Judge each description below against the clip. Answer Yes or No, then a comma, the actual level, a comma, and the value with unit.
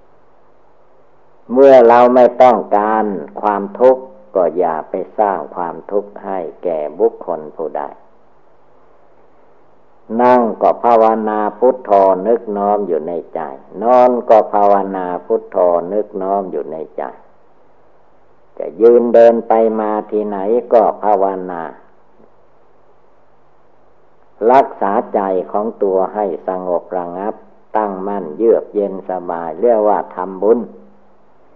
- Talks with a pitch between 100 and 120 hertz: Yes, low, 105 Hz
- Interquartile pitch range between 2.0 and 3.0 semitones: No, average, 3.8 semitones